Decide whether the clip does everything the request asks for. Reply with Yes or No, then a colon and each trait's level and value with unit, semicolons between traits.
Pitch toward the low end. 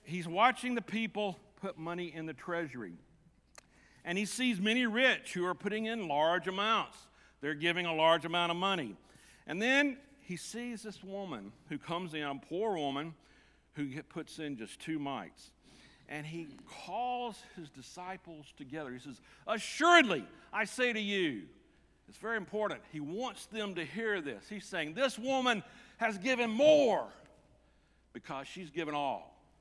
No: medium, 185 Hz